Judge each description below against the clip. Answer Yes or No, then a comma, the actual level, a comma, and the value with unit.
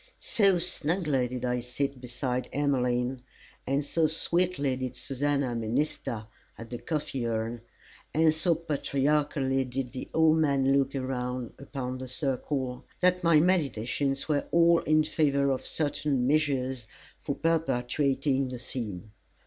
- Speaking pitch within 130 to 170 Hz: Yes, low, 135 Hz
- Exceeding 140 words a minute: No, slow, 135 wpm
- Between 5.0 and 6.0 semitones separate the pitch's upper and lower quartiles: No, average, 3.4 semitones